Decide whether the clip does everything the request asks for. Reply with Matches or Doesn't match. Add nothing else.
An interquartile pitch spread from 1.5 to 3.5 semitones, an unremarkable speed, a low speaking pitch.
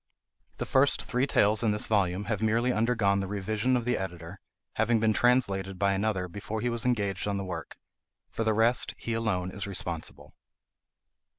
Matches